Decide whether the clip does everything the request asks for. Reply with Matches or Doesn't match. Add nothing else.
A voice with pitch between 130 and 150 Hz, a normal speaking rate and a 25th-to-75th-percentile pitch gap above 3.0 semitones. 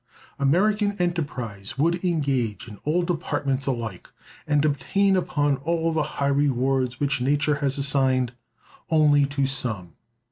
Doesn't match